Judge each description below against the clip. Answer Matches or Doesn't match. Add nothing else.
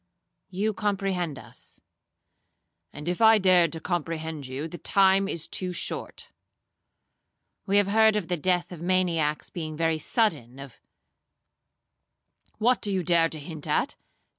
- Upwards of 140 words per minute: Doesn't match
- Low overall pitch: Doesn't match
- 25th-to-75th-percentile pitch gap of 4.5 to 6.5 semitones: Doesn't match